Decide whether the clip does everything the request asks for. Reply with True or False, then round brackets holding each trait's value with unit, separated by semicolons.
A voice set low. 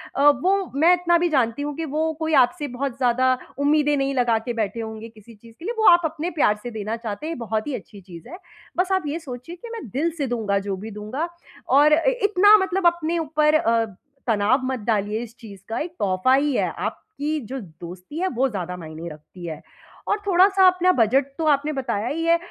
False (270 Hz)